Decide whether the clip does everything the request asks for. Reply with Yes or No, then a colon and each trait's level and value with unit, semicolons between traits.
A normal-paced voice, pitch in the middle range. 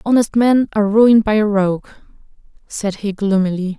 No: average, 160 wpm; high, 210 Hz